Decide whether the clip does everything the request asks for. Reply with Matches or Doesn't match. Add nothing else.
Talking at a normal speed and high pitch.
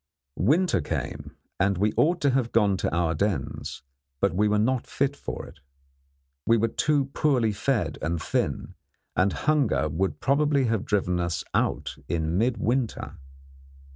Doesn't match